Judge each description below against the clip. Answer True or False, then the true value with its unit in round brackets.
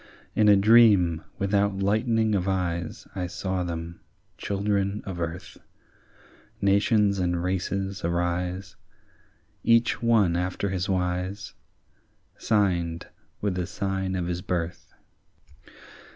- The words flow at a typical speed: False (110 wpm)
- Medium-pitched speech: False (95 Hz)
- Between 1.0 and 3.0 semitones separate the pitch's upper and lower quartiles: True (2.4 semitones)